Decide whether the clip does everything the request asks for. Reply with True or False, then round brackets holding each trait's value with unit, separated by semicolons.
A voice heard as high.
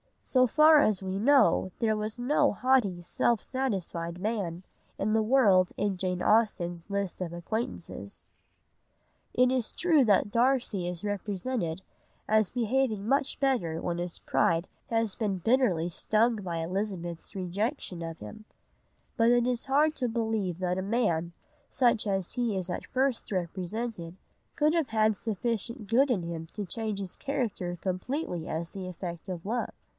True (210 Hz)